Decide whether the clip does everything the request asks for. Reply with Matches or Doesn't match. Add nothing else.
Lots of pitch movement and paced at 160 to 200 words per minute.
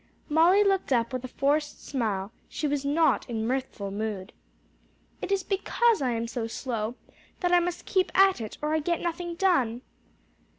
Matches